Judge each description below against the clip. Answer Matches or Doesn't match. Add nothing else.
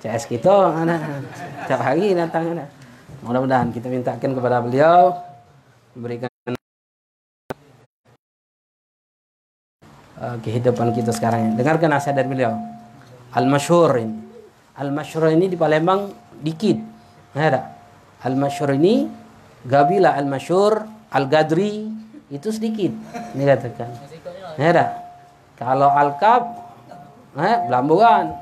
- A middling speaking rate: Matches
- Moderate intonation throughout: Doesn't match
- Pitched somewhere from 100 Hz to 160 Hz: Matches